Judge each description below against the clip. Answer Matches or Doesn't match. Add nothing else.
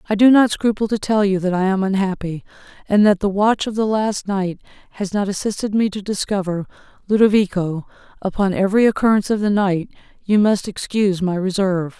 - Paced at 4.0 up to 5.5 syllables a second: Doesn't match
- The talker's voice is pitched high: Matches